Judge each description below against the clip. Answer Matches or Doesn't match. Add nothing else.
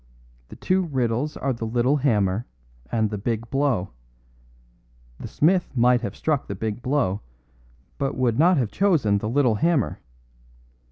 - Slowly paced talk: Doesn't match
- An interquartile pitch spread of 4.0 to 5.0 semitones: Matches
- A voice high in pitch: Doesn't match